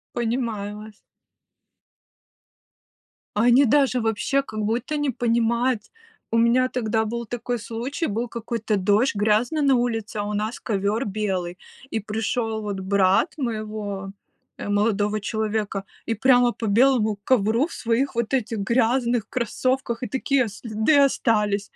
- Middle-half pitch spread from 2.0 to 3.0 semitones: Yes, average, 2.7 semitones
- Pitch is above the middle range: Yes, high, 225 Hz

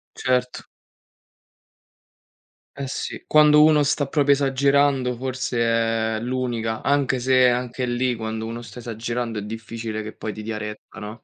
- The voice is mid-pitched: No, low, 125 Hz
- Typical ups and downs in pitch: Yes, average, 3.1 semitones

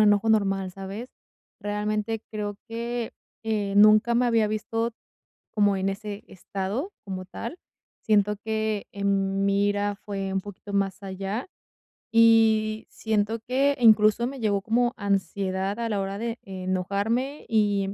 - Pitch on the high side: Yes, high, 210 Hz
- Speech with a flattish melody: Yes, narrow, 2.2 semitones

